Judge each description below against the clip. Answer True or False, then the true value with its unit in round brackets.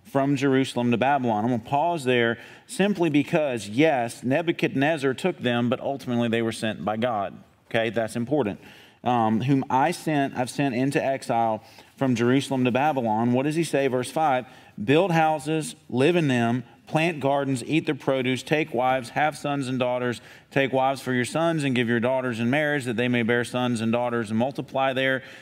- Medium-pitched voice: False (130 Hz)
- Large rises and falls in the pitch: False (3.0 semitones)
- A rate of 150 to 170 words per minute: False (190 wpm)